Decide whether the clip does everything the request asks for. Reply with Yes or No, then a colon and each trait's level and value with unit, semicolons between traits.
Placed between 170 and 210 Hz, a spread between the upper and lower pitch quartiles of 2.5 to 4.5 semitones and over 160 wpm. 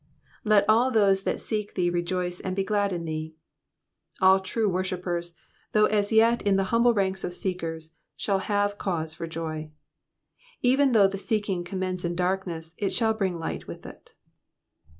Yes: high, 190 Hz; average, 2.9 semitones; average, 170 wpm